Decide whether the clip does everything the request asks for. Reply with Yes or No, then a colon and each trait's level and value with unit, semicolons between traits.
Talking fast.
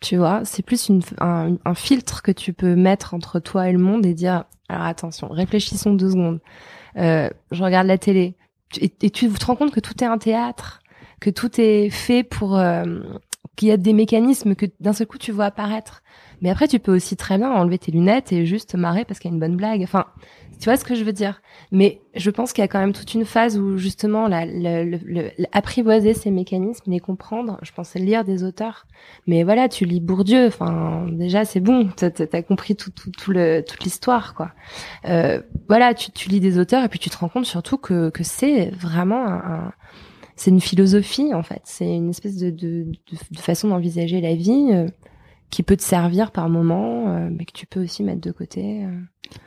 Yes: fast, 225 wpm